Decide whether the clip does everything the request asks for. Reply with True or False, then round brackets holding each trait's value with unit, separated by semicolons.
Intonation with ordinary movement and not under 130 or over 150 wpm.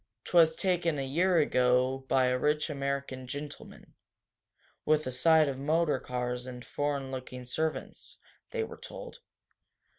True (3.7 semitones; 140 wpm)